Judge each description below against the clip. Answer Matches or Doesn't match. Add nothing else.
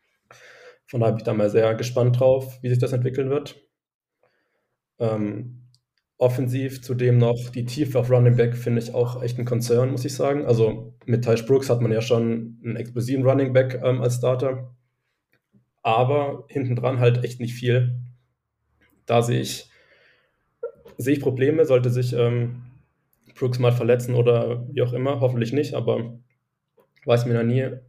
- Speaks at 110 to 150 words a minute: Doesn't match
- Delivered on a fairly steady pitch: Matches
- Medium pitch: Doesn't match